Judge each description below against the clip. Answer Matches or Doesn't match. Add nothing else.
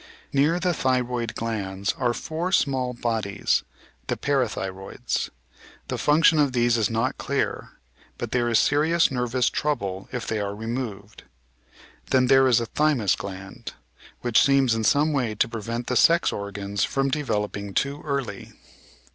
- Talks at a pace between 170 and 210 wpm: Doesn't match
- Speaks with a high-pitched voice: Doesn't match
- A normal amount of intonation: Matches